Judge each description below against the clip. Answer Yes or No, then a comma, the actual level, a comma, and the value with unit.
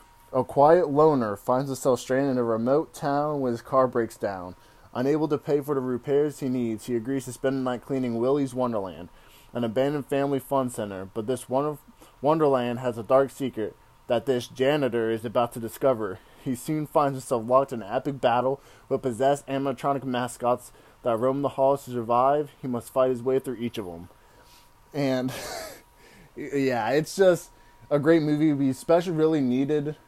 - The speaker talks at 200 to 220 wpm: No, average, 180 wpm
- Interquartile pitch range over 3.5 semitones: No, narrow, 2.6 semitones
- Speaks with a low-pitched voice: Yes, low, 130 Hz